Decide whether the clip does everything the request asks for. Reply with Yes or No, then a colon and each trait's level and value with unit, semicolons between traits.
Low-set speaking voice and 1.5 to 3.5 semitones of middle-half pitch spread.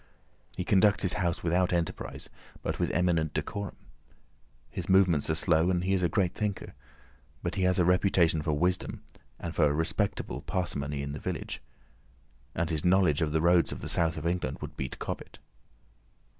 Yes: very low, 85 Hz; narrow, 2.6 semitones